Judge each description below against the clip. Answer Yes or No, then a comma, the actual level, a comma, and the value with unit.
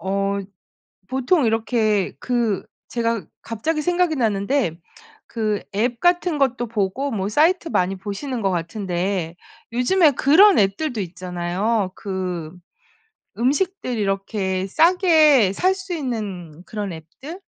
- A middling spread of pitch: No, wide, 6.8 semitones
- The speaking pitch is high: Yes, high, 220 Hz